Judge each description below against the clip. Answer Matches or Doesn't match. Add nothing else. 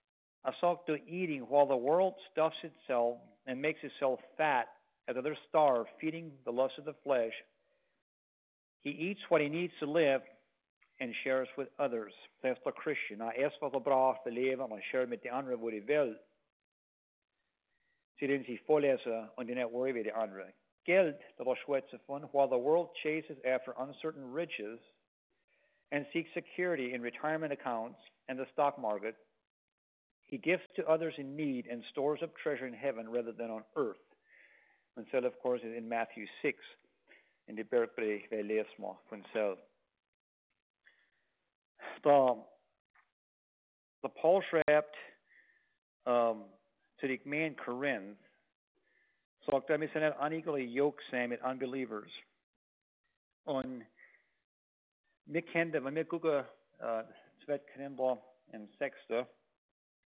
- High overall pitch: Doesn't match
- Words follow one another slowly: Matches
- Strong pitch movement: Doesn't match